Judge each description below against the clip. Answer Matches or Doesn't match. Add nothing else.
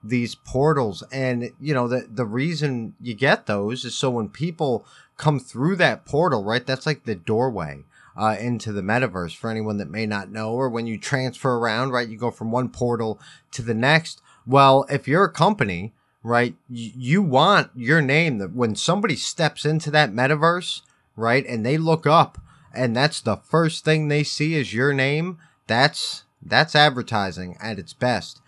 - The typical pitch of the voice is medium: Doesn't match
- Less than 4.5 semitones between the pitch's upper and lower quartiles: Doesn't match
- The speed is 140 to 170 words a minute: Doesn't match